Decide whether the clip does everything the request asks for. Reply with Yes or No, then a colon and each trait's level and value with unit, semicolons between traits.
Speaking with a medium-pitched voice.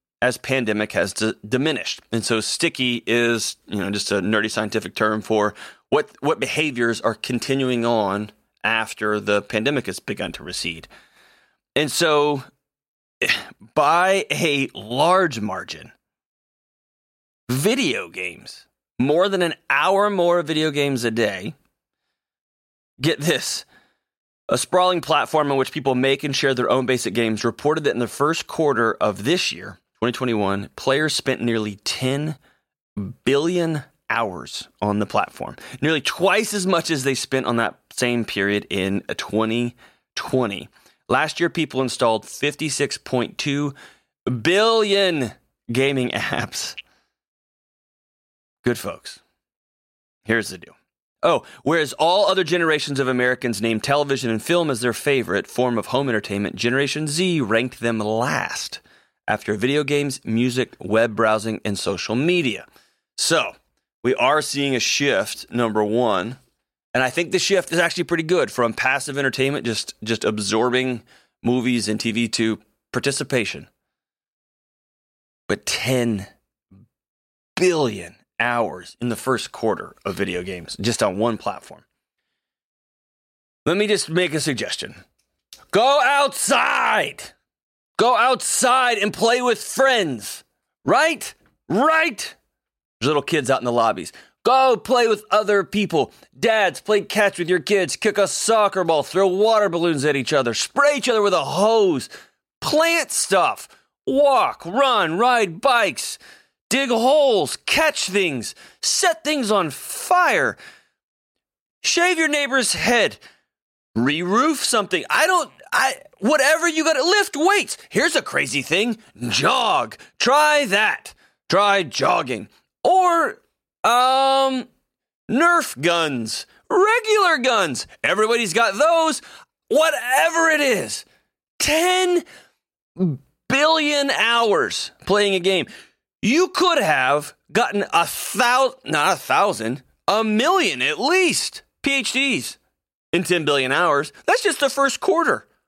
Yes: medium, 150 Hz